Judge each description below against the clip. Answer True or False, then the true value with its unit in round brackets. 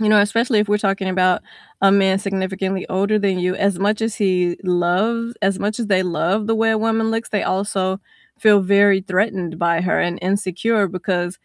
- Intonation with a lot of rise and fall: False (2.4 semitones)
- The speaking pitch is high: True (195 Hz)